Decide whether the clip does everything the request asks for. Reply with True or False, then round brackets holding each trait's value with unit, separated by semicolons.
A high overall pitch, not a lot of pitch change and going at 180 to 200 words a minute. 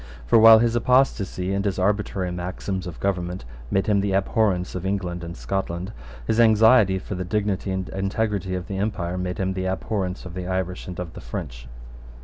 False (95 Hz; 2.3 semitones; 190 wpm)